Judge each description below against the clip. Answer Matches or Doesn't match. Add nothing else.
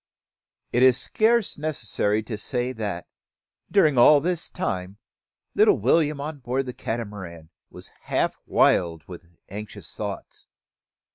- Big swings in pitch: Matches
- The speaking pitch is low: Matches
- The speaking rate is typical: Doesn't match